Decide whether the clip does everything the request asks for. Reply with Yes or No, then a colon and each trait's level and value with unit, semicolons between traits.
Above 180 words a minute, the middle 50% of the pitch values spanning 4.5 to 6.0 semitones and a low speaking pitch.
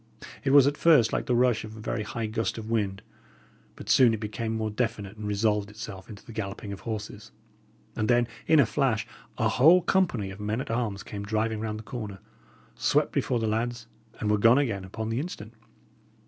No: fast, 205 wpm; narrow, 2.4 semitones; low, 110 Hz